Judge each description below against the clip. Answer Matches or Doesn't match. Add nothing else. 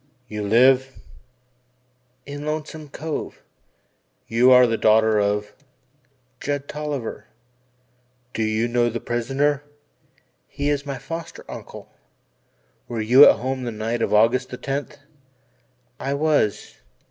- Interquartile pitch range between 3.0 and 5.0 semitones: Matches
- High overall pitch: Doesn't match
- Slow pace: Matches